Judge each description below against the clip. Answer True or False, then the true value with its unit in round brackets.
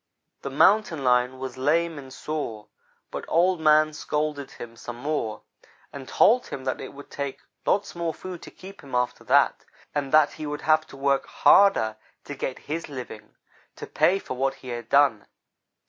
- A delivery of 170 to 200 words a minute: True (180 wpm)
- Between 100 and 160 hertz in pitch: True (140 Hz)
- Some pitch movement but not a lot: True (3.3 semitones)